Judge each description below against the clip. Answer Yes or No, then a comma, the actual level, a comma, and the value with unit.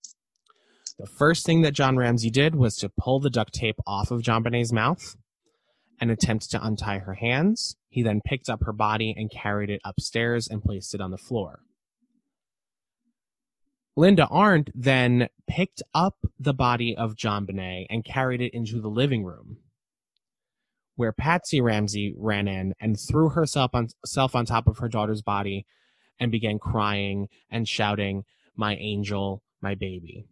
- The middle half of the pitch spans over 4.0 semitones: Yes, average, 4.4 semitones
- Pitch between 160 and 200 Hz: No, low, 115 Hz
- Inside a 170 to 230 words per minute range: No, average, 160 wpm